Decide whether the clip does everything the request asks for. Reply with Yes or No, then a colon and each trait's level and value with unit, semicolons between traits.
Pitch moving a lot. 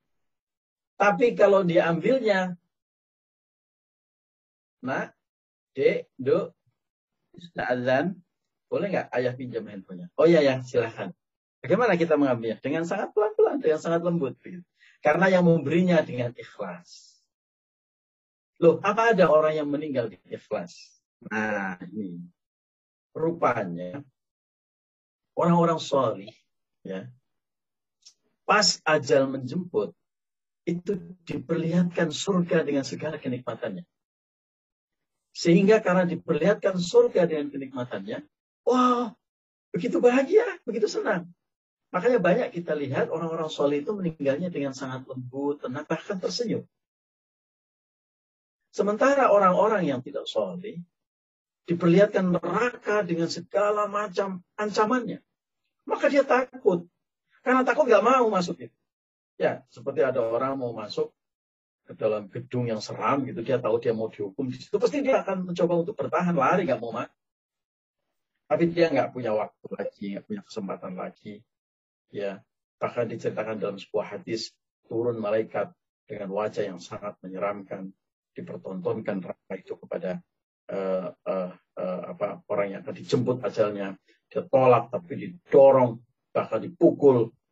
Yes: wide, 8.7 semitones